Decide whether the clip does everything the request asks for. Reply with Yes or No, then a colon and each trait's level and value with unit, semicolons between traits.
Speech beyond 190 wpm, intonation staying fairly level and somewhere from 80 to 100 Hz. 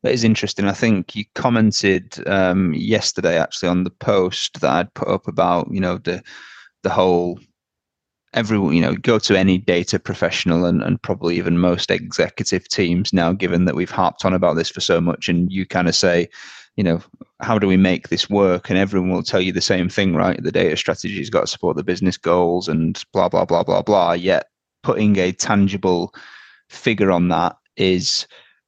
Yes: average, 200 wpm; narrow, 2.0 semitones; very low, 95 Hz